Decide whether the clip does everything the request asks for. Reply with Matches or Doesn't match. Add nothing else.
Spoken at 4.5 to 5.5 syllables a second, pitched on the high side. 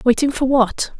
Matches